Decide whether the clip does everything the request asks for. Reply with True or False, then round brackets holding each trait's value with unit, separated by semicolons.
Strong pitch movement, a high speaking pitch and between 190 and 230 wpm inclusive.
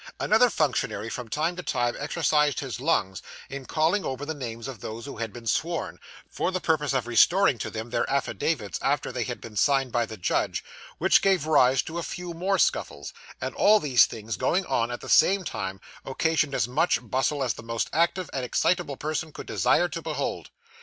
False (5.7 semitones; 140 Hz; 200 wpm)